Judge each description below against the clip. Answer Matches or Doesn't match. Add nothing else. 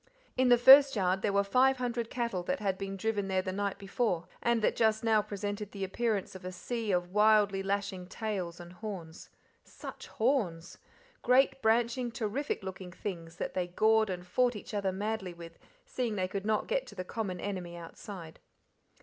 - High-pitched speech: Matches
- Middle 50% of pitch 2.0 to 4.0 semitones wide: Matches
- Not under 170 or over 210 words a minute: Matches